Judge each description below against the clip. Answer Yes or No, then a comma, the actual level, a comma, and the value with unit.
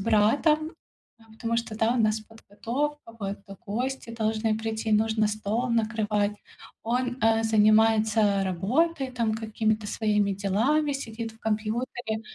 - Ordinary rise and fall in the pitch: No, narrow, 1.6 semitones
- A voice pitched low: No, high, 220 Hz